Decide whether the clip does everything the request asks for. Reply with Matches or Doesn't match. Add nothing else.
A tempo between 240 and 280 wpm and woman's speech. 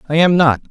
Doesn't match